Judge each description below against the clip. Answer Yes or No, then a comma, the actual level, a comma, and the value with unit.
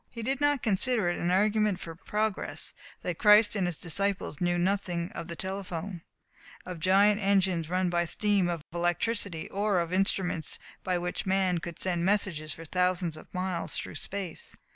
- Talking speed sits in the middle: Yes, average, 170 wpm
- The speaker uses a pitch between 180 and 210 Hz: Yes, medium, 185 Hz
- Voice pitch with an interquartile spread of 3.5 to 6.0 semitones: No, average, 2.7 semitones